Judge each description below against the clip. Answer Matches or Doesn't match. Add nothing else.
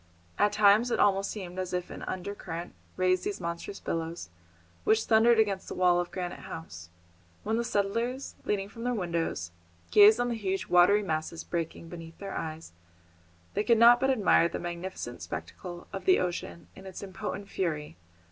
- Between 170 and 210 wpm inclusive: Matches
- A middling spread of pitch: Matches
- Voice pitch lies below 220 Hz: Matches